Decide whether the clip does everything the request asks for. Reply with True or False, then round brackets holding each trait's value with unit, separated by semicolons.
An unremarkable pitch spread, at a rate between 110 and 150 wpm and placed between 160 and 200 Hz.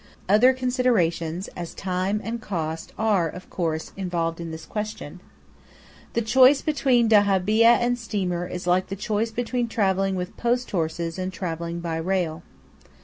True (4.9 semitones; 145 wpm; 190 Hz)